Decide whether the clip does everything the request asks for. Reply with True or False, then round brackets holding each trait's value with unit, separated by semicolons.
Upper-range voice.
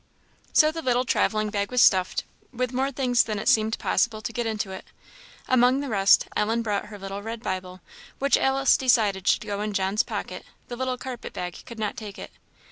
True (220 Hz)